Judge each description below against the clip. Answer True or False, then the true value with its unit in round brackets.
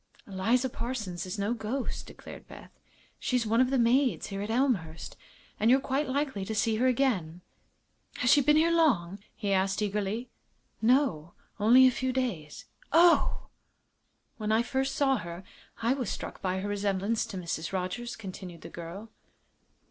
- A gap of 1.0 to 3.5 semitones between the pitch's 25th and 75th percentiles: False (5.3 semitones)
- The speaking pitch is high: True (225 Hz)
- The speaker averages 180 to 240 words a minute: False (165 wpm)